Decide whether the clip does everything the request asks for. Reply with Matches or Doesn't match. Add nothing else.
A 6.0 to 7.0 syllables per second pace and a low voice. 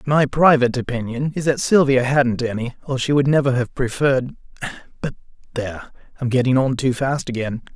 Doesn't match